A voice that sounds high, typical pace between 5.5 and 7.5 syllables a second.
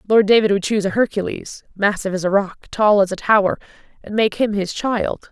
Yes: high, 200 Hz; 5.7 syllables/s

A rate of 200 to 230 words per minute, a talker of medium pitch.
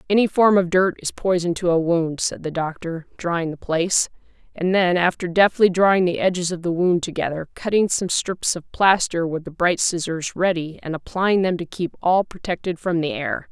Yes: fast, 205 wpm; medium, 175 Hz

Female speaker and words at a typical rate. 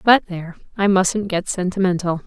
Yes: female; average, 160 wpm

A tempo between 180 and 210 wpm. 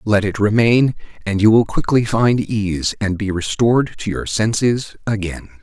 No: average, 170 wpm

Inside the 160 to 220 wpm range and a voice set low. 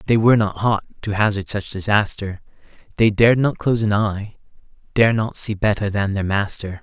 Yes: average, 175 wpm; low, 105 Hz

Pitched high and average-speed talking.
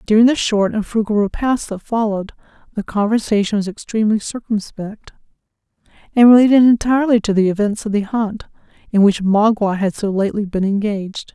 Yes: high, 210 Hz; average, 160 wpm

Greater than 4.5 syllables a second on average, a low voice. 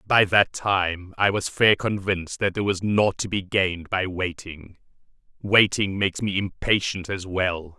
No: 4.4 syllables/s; very low, 95 Hz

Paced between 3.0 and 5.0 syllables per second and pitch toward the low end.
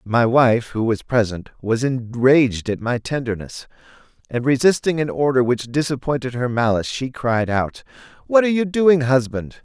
Yes: 4.8 syllables/s; low, 130 Hz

